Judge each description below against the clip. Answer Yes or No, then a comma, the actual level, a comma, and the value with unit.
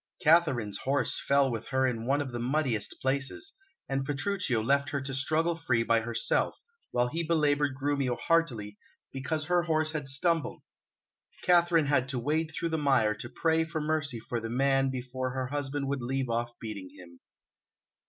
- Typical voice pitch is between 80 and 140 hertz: Yes, low, 135 Hz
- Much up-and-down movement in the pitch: No, average, 4.2 semitones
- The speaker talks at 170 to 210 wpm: Yes, average, 175 wpm